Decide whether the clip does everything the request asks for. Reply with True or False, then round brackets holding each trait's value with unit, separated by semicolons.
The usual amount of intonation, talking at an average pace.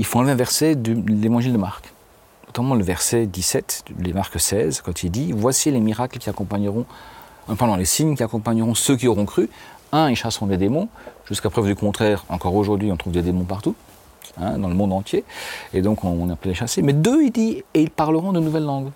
False (4.4 semitones; 225 wpm)